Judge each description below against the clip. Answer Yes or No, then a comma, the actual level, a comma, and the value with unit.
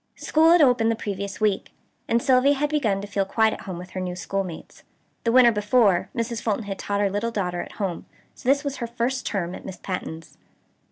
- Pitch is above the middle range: Yes, high, 210 Hz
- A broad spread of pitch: No, average, 4.1 semitones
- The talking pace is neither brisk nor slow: No, fast, 220 wpm